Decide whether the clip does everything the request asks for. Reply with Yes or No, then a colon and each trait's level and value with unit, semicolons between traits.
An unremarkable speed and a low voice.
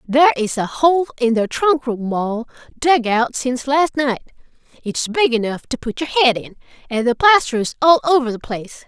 No: average, 195 wpm; very high, 260 Hz